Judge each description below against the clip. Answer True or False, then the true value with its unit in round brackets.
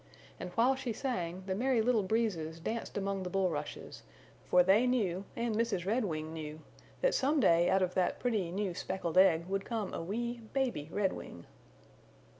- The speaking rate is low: False (170 wpm)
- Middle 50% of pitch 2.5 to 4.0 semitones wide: False (4.9 semitones)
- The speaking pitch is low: False (195 Hz)